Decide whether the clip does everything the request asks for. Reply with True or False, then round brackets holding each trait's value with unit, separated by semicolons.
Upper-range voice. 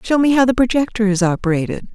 True (225 Hz)